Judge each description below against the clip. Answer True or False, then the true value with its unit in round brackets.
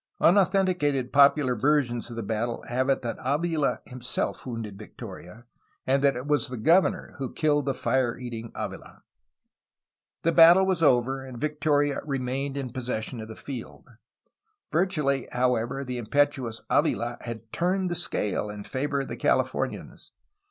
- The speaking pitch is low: True (130 Hz)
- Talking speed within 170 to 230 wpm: False (150 wpm)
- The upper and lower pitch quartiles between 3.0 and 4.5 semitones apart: True (3.6 semitones)